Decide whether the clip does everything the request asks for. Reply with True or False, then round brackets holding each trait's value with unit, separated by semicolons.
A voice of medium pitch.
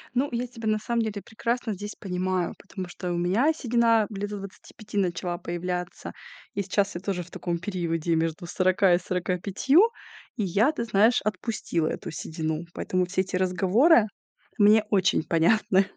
False (195 Hz)